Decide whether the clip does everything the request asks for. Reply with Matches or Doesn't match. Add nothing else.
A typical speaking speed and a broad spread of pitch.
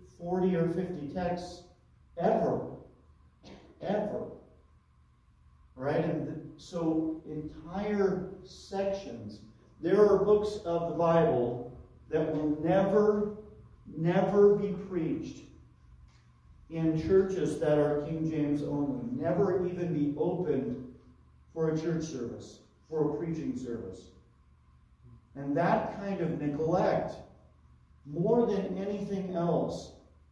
Doesn't match